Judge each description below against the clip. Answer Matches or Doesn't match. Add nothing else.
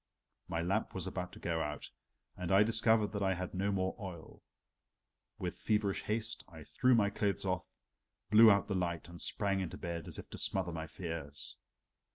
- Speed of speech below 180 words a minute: Doesn't match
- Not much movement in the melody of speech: Doesn't match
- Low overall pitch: Matches